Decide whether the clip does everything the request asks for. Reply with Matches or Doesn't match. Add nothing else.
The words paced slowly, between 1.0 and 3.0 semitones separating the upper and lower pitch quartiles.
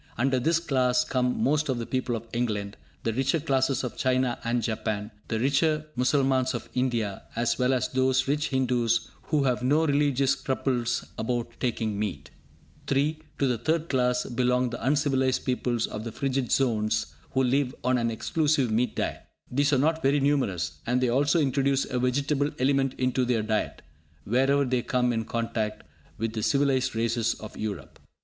Doesn't match